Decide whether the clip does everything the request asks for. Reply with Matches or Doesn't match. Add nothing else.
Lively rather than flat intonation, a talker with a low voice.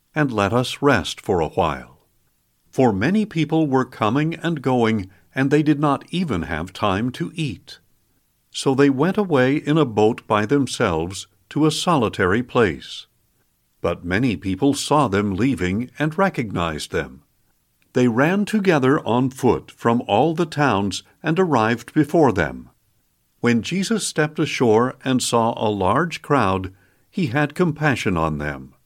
Matches